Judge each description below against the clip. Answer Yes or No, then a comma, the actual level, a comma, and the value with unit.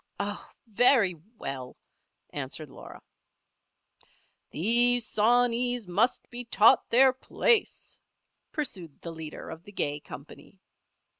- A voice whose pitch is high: Yes, high, 210 Hz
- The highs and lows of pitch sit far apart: Yes, wide, 7.1 semitones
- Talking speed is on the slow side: Yes, slow, 100 wpm